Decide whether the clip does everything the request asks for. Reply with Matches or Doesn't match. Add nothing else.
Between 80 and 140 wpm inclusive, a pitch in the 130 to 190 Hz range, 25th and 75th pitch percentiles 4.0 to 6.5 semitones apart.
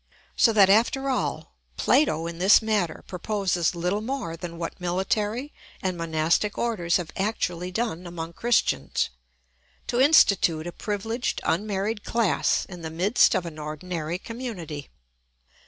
Matches